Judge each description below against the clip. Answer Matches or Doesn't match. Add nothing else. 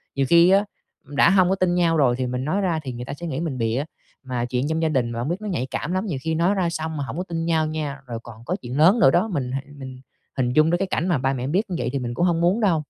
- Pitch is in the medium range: Matches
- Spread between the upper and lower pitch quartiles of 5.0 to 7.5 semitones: Matches